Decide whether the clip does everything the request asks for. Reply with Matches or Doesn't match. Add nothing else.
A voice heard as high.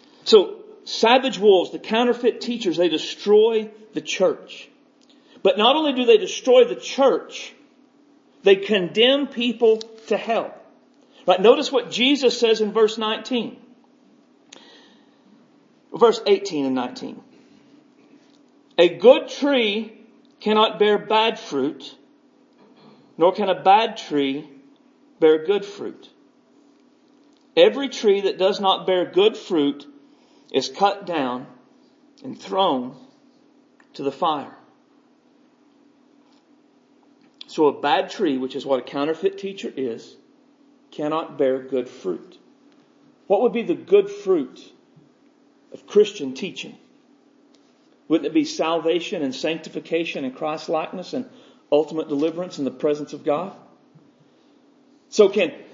Matches